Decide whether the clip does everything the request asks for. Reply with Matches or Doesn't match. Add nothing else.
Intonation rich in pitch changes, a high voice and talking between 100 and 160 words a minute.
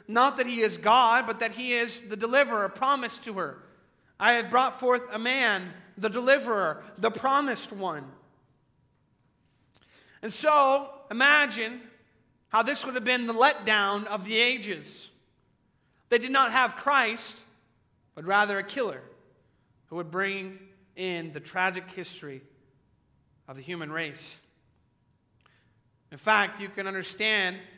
Matches